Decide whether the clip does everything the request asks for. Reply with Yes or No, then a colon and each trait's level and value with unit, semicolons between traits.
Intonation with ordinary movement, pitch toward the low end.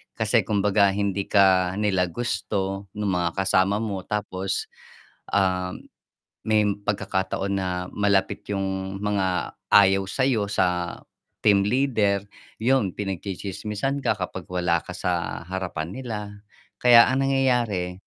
No: narrow, 2.1 semitones; low, 100 Hz